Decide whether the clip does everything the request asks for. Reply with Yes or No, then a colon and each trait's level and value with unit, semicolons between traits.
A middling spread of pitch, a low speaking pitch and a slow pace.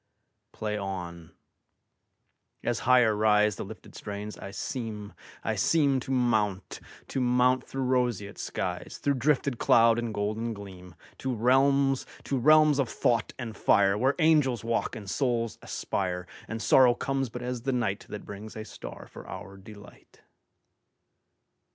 Yes: average, 3.8 semitones; low, 115 Hz; slow, 125 wpm